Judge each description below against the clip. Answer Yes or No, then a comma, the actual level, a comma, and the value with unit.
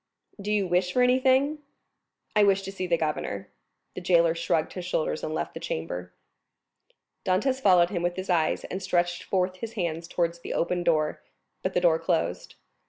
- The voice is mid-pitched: Yes, medium, 180 Hz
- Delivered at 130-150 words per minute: No, average, 180 wpm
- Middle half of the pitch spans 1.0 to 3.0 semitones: Yes, narrow, 2.6 semitones